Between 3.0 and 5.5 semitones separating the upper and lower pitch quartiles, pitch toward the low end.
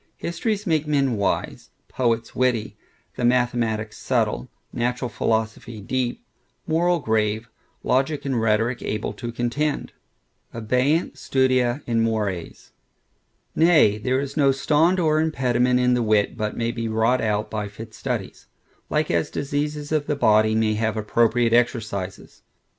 Yes: average, 3.9 semitones; low, 120 Hz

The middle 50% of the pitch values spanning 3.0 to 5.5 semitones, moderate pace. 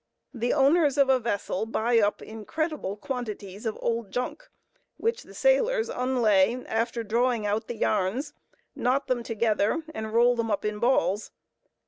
Yes: average, 3.6 semitones; average, 150 wpm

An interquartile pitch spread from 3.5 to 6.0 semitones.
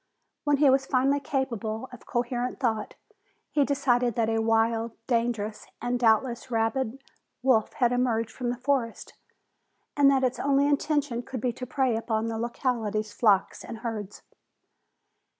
No: average, 2.9 semitones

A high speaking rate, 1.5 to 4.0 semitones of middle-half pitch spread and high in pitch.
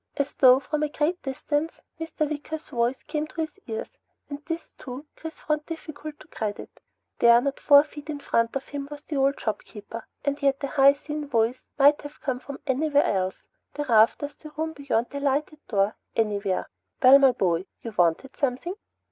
No: average, 190 wpm; average, 3.5 semitones; very high, 280 Hz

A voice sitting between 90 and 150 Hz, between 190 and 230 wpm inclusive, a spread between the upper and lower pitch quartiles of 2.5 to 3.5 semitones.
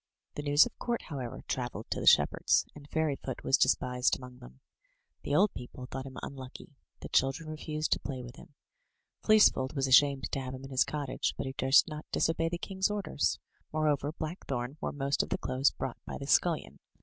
Yes: medium, 140 Hz; average, 200 wpm; average, 2.9 semitones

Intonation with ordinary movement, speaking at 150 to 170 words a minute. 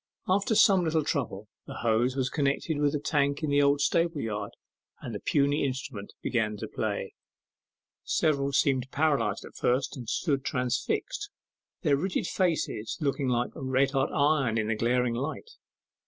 Yes: average, 3.7 semitones; average, 160 wpm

